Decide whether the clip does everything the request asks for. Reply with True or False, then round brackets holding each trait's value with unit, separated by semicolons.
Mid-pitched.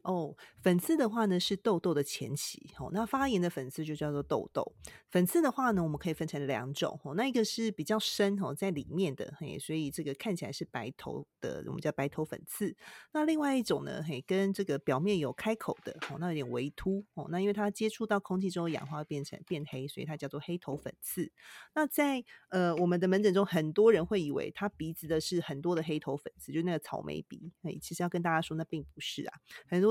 True (175 Hz)